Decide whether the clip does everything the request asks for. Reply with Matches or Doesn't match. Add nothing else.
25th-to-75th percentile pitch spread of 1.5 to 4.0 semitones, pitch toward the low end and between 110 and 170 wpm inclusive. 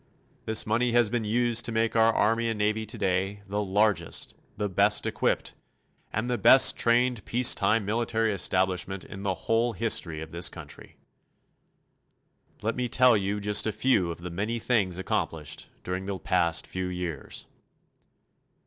Matches